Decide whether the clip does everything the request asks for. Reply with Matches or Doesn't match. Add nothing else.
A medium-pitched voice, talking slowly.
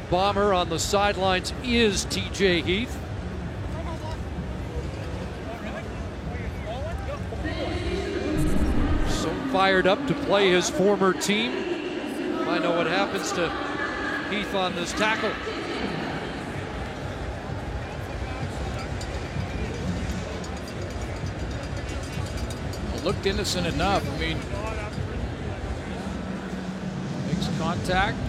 Matches